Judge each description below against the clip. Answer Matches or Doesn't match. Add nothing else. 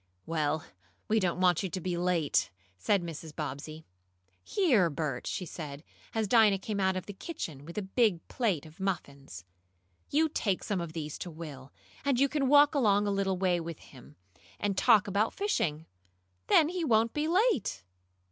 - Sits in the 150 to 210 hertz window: Matches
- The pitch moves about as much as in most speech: Doesn't match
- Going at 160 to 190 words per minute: Matches